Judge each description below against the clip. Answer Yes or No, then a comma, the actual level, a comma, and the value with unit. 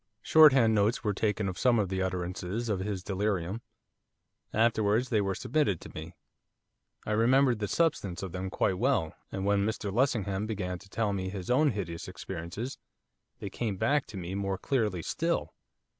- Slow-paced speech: No, average, 175 wpm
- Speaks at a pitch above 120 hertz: No, low, 100 Hz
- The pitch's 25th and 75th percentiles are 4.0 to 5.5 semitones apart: No, average, 3.5 semitones